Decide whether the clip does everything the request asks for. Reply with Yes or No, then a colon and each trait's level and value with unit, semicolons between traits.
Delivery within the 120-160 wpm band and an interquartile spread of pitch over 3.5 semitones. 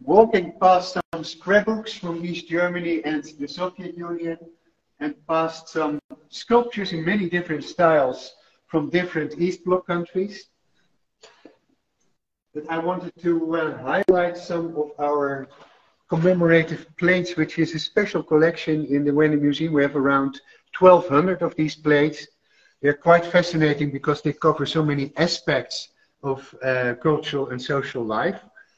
No: average, 140 wpm; average, 2.9 semitones